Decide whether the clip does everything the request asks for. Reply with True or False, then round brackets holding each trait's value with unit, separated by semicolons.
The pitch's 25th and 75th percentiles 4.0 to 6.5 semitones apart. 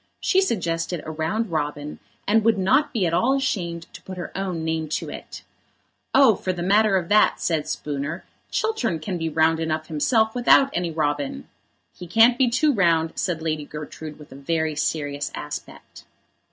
True (5.6 semitones)